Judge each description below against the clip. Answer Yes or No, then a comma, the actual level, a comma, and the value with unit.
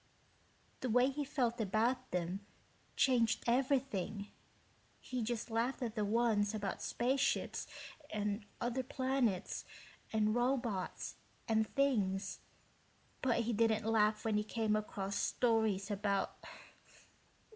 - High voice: Yes, high, 225 Hz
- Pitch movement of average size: Yes, average, 3.0 semitones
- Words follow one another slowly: Yes, slow, 115 wpm